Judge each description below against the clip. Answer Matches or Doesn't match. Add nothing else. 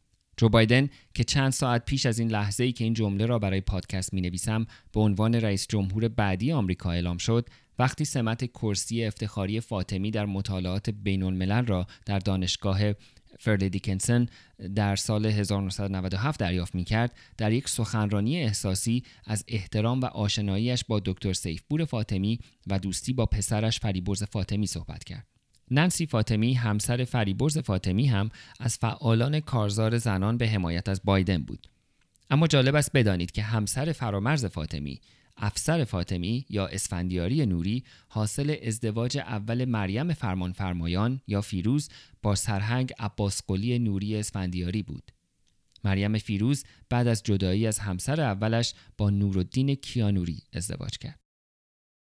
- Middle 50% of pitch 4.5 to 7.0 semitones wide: Doesn't match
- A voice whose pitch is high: Doesn't match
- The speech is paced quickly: Doesn't match